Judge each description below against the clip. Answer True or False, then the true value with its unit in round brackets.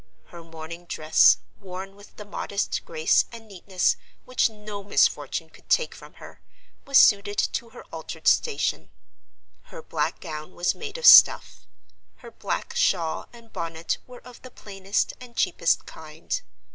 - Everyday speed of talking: True (150 wpm)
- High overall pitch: True (205 Hz)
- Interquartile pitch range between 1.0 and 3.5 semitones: False (5.4 semitones)